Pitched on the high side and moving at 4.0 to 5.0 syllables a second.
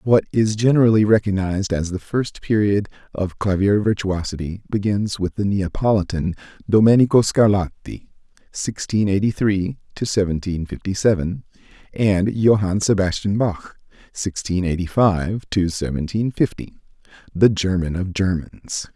No: low, 100 Hz; 4.5 syllables/s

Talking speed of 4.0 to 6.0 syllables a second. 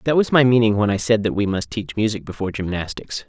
No: 6.4 syllables/s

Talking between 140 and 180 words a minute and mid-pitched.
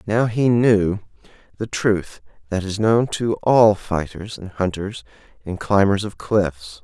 No: average, 150 wpm; low, 100 Hz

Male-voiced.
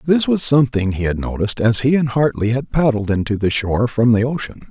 Yes: male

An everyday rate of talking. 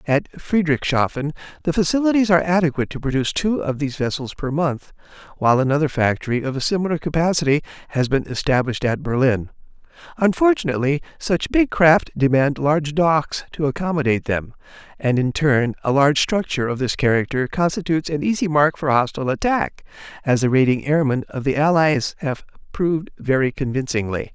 Yes: average, 155 wpm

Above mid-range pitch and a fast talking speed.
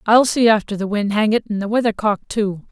Yes: high, 215 Hz; fast, 265 wpm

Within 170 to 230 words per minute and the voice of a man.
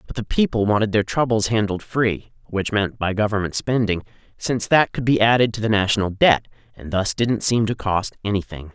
Yes: average, 190 wpm; male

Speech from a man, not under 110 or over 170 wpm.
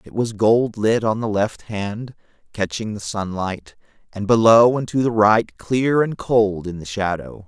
No: male; average, 185 wpm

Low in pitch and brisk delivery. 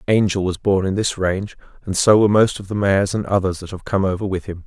Yes: low, 100 Hz; fast, 270 wpm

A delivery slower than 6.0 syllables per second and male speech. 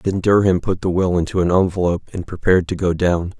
No: 6.2 syllables/s; male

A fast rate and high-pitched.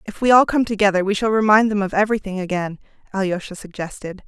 No: average, 195 wpm; high, 200 Hz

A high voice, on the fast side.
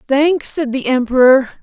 No: very high, 270 Hz; average, 150 wpm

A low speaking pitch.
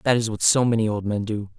Yes: low, 110 Hz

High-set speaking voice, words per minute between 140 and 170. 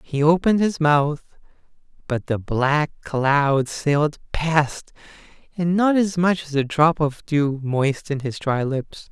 No: medium, 150 Hz; average, 150 wpm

